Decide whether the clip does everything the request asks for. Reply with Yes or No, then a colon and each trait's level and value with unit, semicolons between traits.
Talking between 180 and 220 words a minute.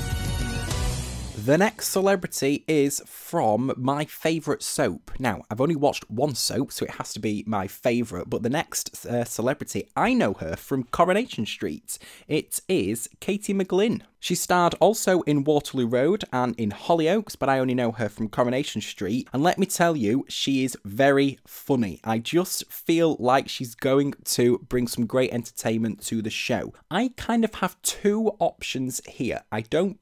No: average, 170 wpm